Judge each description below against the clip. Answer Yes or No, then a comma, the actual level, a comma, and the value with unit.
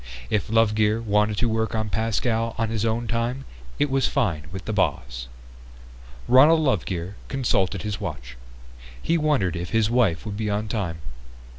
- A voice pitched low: Yes, low, 110 Hz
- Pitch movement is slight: No, average, 3.2 semitones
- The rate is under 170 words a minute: Yes, average, 160 wpm